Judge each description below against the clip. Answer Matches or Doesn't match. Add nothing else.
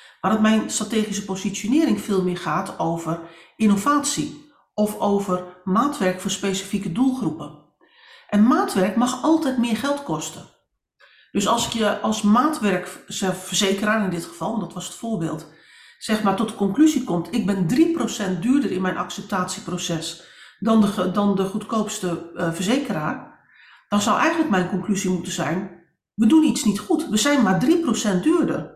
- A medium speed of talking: Matches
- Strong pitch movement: Doesn't match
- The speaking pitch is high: Matches